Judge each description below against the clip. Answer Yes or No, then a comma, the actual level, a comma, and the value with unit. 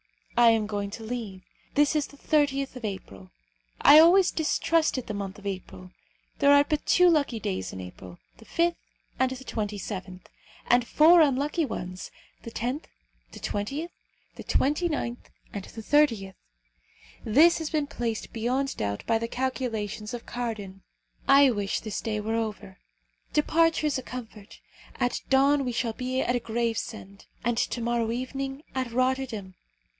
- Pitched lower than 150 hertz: No, high, 240 Hz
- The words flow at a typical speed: Yes, average, 155 wpm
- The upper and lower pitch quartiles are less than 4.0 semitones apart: No, average, 5.0 semitones